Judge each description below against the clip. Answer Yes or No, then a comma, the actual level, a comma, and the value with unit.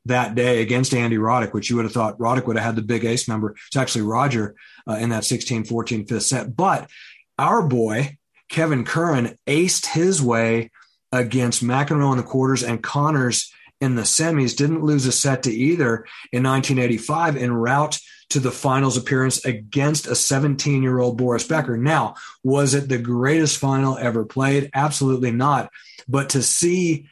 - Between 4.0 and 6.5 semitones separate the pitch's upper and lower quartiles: No, average, 3.1 semitones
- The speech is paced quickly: No, average, 170 wpm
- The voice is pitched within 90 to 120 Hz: No, low, 130 Hz